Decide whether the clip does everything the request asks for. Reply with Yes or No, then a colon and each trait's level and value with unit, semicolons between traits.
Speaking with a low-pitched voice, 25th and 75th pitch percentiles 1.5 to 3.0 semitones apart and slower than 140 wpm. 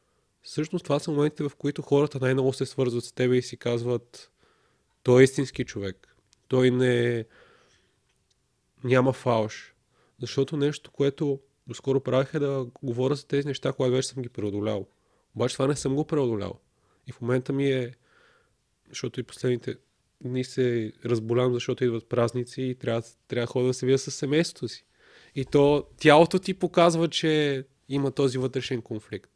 No: low, 130 Hz; narrow, 2.6 semitones; fast, 165 wpm